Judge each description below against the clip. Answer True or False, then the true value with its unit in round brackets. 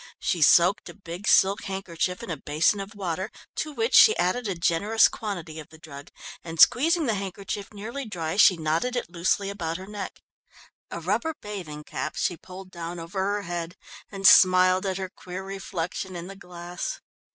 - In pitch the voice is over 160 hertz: True (185 Hz)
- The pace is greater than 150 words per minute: True (185 wpm)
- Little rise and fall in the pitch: False (3.1 semitones)